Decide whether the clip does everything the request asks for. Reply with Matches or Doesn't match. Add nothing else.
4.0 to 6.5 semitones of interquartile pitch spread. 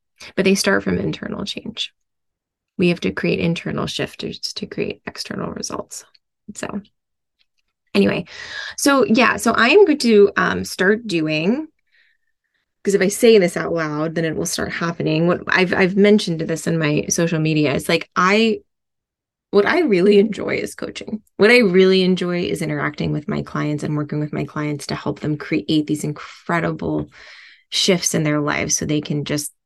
Matches